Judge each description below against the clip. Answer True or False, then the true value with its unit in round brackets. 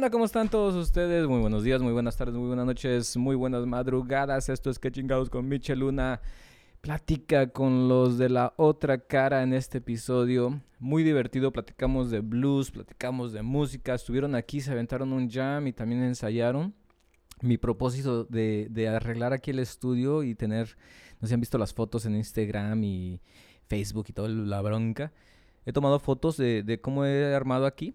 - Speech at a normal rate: True (180 wpm)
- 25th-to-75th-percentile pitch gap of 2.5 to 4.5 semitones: True (2.9 semitones)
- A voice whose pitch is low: True (125 Hz)